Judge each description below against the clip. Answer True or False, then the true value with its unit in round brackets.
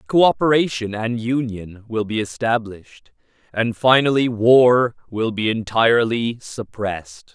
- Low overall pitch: True (115 Hz)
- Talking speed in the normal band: False (105 wpm)